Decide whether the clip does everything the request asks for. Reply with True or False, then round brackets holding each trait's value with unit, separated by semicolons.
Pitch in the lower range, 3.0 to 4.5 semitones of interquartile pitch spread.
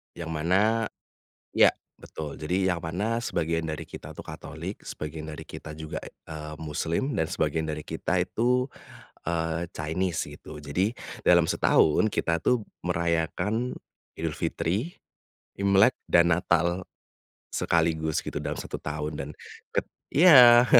True (85 Hz; 3.3 semitones)